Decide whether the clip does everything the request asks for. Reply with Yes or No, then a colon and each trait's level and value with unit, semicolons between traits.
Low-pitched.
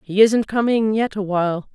No: high, 205 Hz